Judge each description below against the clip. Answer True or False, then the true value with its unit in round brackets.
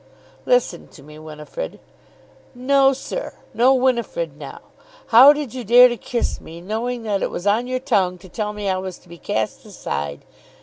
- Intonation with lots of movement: True (5.7 semitones)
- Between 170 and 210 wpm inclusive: True (180 wpm)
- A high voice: True (230 Hz)